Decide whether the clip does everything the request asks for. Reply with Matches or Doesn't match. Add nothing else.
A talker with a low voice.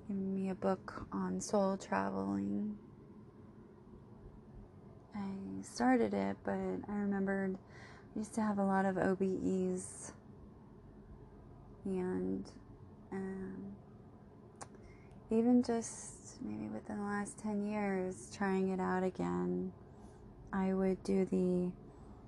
Doesn't match